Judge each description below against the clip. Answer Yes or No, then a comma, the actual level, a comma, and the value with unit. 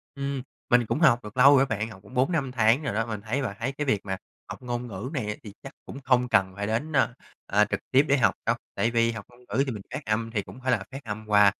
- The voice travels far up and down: No, average, 4.0 semitones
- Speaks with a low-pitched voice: Yes, low, 120 Hz